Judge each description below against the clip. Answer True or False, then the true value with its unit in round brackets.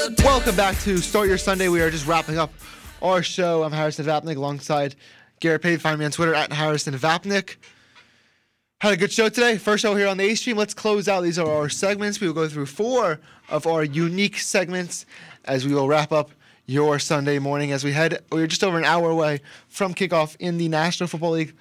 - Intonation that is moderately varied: True (4.2 semitones)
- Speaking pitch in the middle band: True (165 Hz)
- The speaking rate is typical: False (215 wpm)